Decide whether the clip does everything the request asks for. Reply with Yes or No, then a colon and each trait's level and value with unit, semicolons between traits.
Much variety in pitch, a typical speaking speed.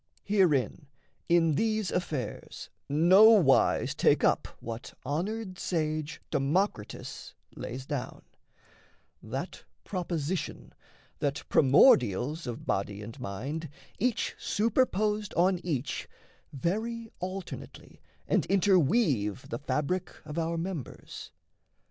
No: wide, 5.9 semitones; slow, 95 wpm